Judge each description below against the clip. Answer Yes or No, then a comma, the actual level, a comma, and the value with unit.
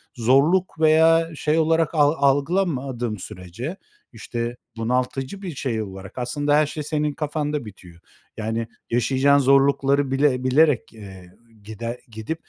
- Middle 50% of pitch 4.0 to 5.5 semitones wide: Yes, average, 4.6 semitones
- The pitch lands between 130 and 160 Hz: Yes, low, 135 Hz